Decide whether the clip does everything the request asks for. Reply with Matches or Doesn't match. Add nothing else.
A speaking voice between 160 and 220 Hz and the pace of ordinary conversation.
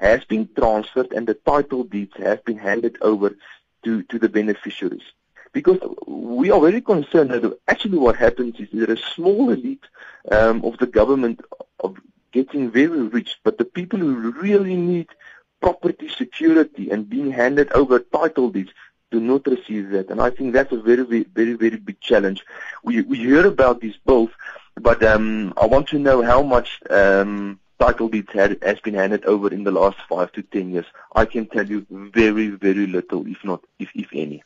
Doesn't match